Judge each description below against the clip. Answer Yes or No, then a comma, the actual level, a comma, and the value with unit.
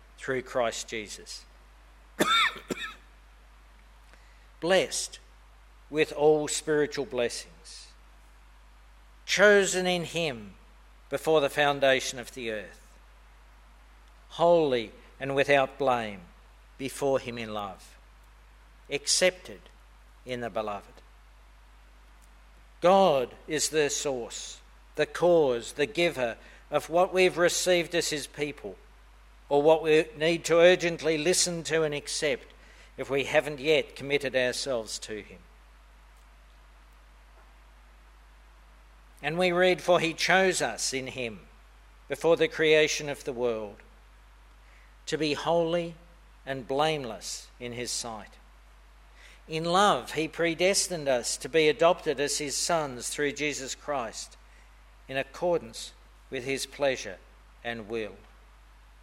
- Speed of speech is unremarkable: No, slow, 110 wpm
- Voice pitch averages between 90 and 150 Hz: Yes, low, 135 Hz